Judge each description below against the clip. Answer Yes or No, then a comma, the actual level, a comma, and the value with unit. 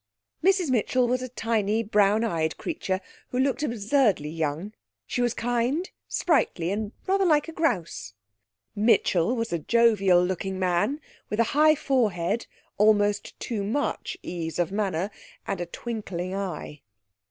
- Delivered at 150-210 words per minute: No, average, 140 wpm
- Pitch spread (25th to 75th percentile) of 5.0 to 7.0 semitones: Yes, average, 5.3 semitones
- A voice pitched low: No, high, 215 Hz